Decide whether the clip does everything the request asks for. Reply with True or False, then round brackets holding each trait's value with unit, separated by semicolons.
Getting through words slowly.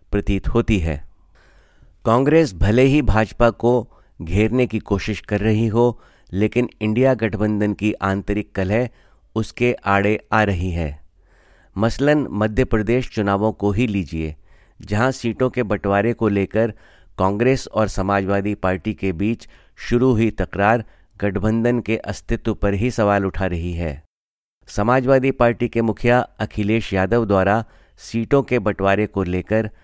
False (135 wpm)